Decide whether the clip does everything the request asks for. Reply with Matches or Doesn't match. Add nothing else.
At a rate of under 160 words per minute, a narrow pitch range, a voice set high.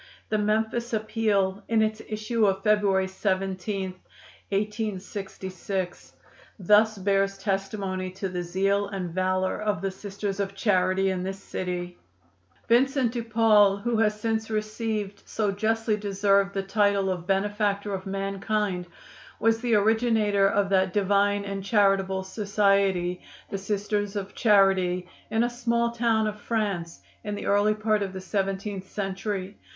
Matches